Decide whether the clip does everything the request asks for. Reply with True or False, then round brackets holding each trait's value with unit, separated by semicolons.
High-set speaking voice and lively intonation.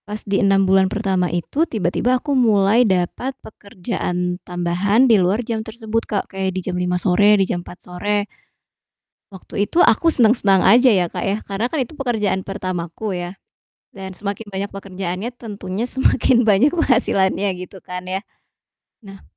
False (195 Hz; 3.2 semitones)